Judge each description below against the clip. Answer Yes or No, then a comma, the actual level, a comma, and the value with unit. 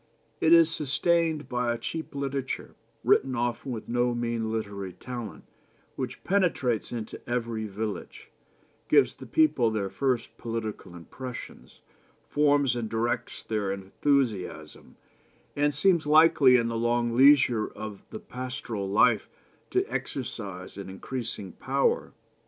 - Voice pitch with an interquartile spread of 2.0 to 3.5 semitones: No, average, 4.2 semitones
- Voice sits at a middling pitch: No, low, 120 Hz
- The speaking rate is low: Yes, slow, 125 wpm